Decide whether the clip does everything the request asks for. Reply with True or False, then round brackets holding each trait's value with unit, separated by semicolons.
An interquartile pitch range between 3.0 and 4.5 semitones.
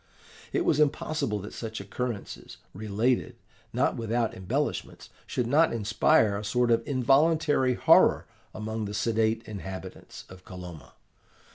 True (3.5 semitones)